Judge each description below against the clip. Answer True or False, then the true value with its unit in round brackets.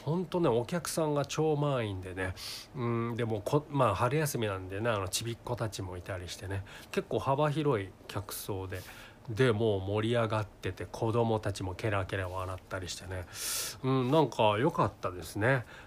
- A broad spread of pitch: False (4.8 semitones)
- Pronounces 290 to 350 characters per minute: True (335 characters per minute)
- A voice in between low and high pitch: False (110 Hz)